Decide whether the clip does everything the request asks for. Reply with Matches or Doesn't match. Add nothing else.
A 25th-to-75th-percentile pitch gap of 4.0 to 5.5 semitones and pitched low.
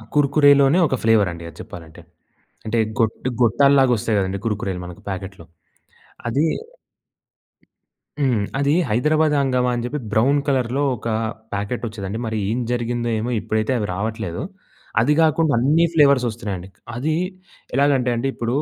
Matches